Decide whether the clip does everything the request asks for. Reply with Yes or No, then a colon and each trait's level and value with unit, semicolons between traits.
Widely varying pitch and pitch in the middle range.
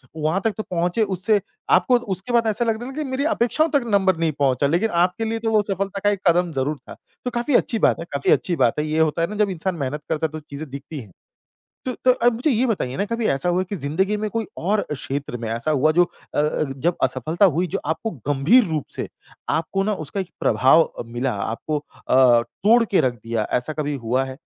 Yes: wide, 7.0 semitones; medium, 175 Hz